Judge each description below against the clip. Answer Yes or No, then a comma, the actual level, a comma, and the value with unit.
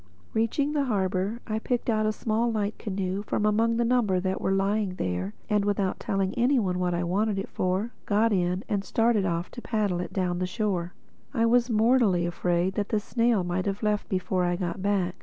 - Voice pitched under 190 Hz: No, high, 200 Hz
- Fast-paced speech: Yes, fast, 210 wpm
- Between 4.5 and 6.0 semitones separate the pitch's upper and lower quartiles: No, average, 3.4 semitones